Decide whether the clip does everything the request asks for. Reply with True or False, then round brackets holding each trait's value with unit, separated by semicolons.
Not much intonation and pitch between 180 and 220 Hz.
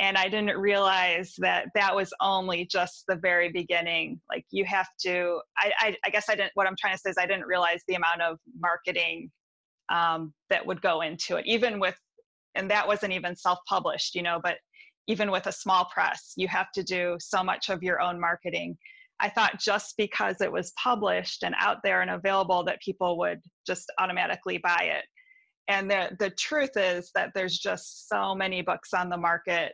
True (2.2 semitones; 185 Hz)